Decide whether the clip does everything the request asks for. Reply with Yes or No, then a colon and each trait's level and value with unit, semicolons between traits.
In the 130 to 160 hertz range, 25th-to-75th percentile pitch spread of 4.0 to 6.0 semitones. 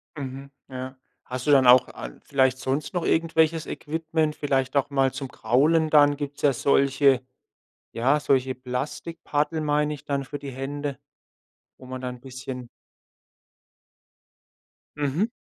No: medium, 140 Hz; narrow, 2.4 semitones